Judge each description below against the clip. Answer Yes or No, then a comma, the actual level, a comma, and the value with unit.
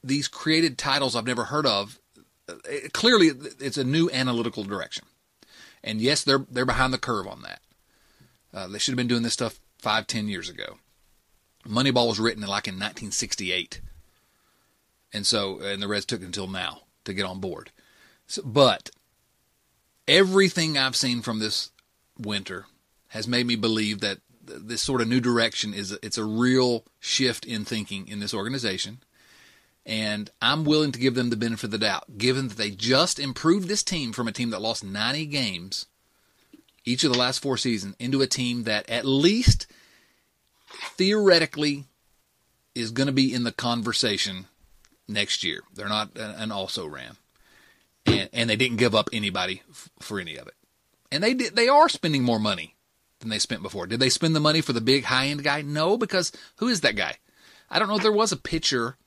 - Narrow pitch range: No, average, 4.4 semitones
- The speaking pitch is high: No, low, 120 Hz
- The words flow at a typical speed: Yes, average, 180 wpm